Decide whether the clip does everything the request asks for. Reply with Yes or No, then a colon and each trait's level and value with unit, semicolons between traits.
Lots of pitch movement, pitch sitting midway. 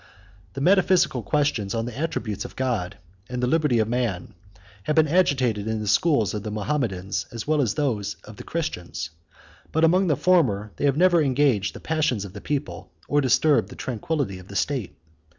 No: wide, 6.4 semitones; low, 125 Hz